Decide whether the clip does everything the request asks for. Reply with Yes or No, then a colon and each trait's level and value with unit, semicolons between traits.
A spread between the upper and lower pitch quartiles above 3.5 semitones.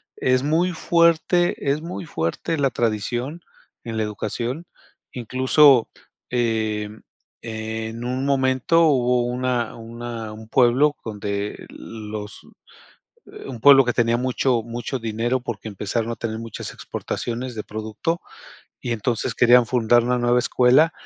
No: average, 2.8 semitones